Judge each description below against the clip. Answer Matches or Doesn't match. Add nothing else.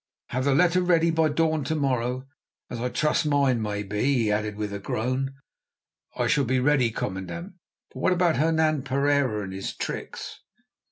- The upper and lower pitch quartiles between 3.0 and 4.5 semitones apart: Doesn't match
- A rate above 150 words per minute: Matches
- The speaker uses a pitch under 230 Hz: Matches